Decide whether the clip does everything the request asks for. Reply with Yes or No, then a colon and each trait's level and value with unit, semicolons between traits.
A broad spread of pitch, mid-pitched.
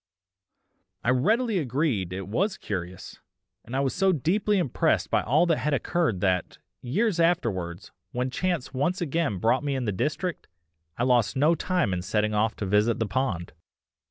No: wide, 8.3 semitones; low, 130 Hz